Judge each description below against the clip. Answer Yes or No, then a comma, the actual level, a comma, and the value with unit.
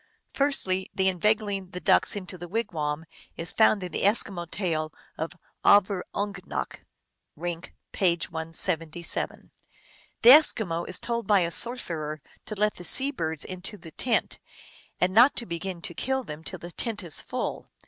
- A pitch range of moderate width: Yes, average, 4.0 semitones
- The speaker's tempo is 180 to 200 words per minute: No, average, 155 wpm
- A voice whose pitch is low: No, medium, 185 Hz